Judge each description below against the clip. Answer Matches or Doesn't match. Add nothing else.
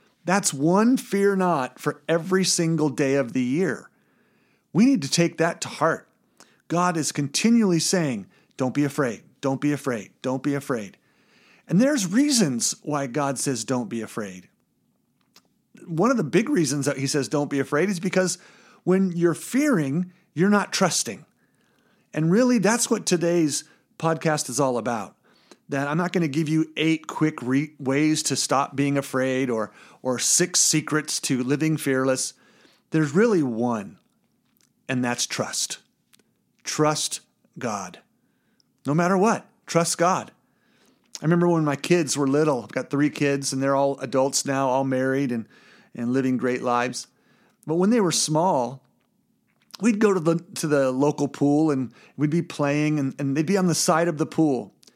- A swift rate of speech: Doesn't match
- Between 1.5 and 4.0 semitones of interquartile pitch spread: Doesn't match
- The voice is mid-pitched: Matches